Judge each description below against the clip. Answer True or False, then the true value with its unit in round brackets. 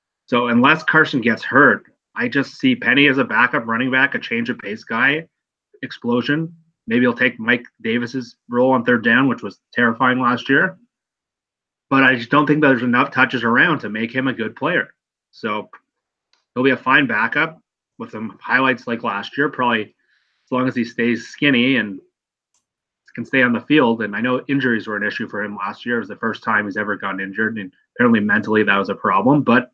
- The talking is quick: True (210 wpm)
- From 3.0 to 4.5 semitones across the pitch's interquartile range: True (4.1 semitones)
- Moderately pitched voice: False (125 Hz)